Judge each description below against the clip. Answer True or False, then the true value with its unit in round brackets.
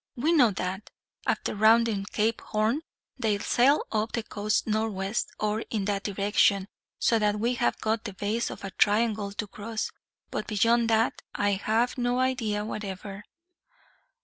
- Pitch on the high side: True (215 Hz)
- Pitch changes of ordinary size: False (2.1 semitones)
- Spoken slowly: False (155 wpm)